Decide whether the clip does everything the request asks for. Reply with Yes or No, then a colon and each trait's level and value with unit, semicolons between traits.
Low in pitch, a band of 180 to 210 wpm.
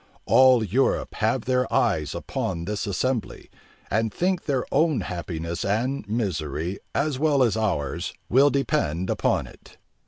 No: low, 110 Hz; slow, 135 wpm